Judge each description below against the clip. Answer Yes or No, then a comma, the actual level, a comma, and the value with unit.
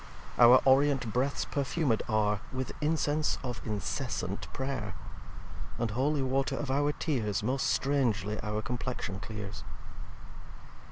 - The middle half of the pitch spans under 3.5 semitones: No, average, 4.4 semitones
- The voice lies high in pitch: No, low, 125 Hz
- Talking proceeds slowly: Yes, slow, 115 wpm